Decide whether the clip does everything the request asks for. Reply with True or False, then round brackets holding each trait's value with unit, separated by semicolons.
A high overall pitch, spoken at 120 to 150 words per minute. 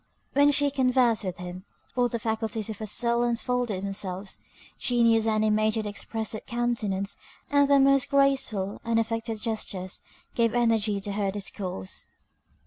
True (225 Hz; 135 wpm)